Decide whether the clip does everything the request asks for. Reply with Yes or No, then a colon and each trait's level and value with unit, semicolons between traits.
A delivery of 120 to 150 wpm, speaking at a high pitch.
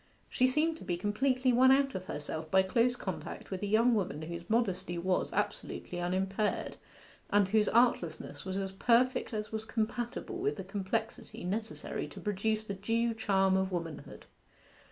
No: average, 165 wpm; high, 205 Hz